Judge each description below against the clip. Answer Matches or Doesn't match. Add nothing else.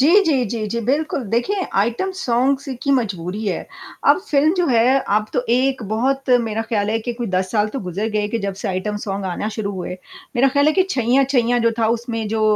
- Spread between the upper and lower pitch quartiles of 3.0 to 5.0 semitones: Matches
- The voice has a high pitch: Matches